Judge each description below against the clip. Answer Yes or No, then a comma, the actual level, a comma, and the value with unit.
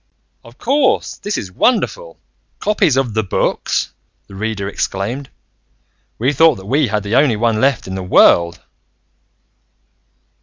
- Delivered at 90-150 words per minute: Yes, average, 140 wpm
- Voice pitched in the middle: No, low, 115 Hz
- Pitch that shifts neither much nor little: No, wide, 6.6 semitones